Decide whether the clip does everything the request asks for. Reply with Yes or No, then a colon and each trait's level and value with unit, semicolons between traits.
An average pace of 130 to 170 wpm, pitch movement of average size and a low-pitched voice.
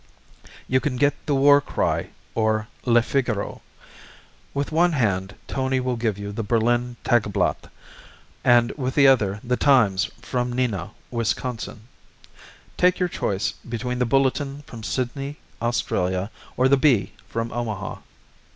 Yes: slow, 135 wpm; average, 3.6 semitones; low, 120 Hz